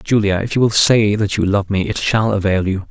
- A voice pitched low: Yes, low, 105 Hz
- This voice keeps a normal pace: No, fast, 270 wpm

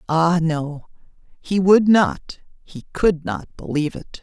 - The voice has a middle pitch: Yes, medium, 170 Hz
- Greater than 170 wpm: No, average, 140 wpm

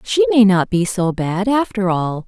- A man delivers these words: No, female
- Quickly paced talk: Yes, fast, 210 wpm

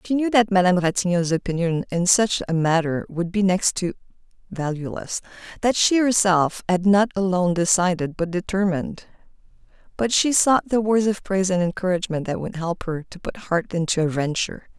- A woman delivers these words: Yes, female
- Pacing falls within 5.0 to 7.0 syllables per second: Yes, 5.5 syllables/s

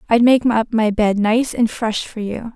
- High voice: Yes, high, 225 Hz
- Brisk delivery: Yes, fast, 235 wpm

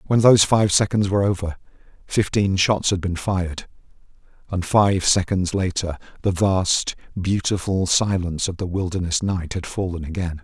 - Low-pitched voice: Yes, very low, 95 Hz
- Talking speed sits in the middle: Yes, average, 150 wpm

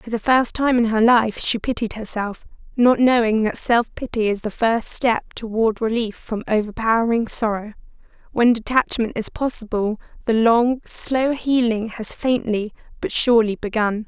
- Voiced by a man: No, female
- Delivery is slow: No, average, 160 wpm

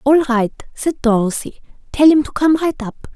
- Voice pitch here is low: No, very high, 270 Hz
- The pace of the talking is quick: No, average, 190 wpm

